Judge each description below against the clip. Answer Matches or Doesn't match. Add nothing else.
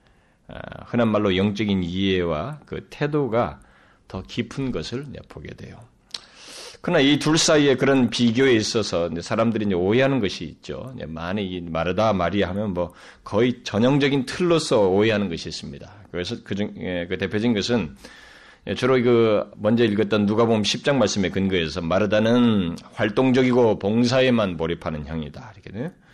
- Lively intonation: Doesn't match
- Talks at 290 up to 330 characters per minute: Matches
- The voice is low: Matches